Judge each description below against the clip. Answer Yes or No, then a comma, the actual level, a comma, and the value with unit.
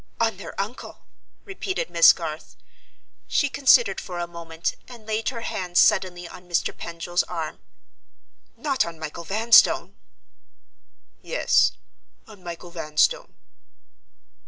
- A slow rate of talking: Yes, slow, 115 wpm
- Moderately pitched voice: Yes, medium, 180 Hz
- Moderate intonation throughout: Yes, average, 5.0 semitones